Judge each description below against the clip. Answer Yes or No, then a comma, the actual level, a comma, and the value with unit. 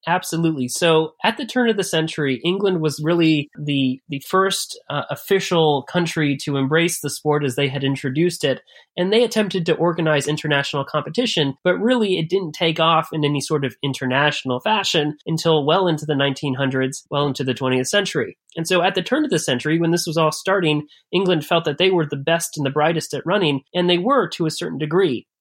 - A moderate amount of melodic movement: Yes, average, 3.7 semitones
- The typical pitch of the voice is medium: Yes, medium, 160 Hz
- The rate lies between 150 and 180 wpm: No, fast, 205 wpm